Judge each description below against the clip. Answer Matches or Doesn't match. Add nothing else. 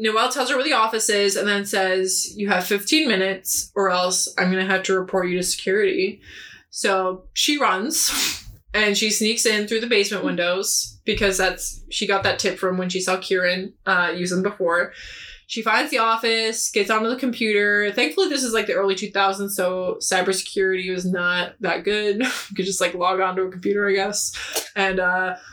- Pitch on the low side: Doesn't match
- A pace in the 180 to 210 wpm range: Matches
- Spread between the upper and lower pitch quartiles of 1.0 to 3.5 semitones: Matches